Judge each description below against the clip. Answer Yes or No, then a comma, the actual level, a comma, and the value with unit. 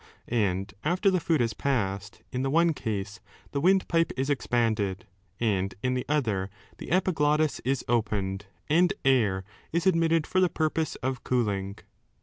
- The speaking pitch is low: Yes, low, 130 Hz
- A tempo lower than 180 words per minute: Yes, average, 150 wpm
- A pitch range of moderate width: No, wide, 7.6 semitones